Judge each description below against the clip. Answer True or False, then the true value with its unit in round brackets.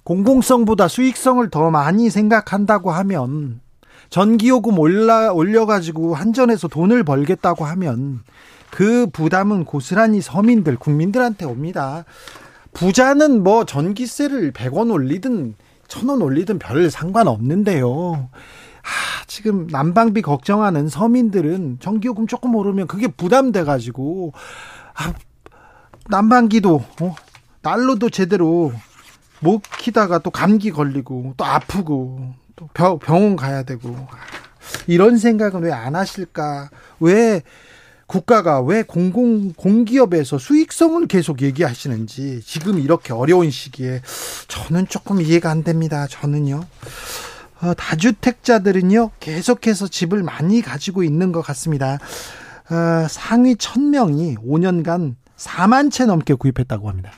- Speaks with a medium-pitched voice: True (180 Hz)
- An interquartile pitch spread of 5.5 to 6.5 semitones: False (7.3 semitones)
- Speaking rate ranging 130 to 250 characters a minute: False (260 characters per minute)